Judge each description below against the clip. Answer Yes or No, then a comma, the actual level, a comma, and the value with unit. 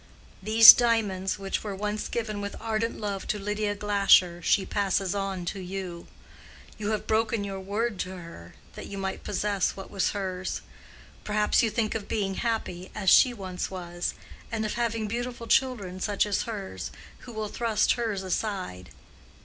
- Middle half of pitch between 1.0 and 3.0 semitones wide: Yes, narrow, 2.5 semitones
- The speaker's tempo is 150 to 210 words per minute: Yes, average, 165 wpm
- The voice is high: Yes, high, 205 Hz